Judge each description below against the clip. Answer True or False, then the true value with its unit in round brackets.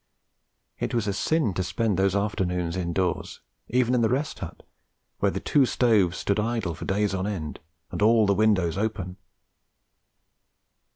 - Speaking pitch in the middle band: False (100 Hz)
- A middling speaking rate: True (160 wpm)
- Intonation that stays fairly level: False (3.5 semitones)